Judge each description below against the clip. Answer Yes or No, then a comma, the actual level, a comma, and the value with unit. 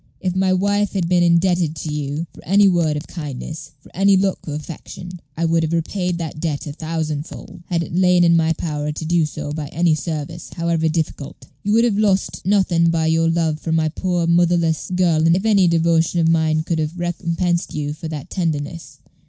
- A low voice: No, medium, 165 Hz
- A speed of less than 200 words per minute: No, fast, 205 wpm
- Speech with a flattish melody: Yes, narrow, 2.1 semitones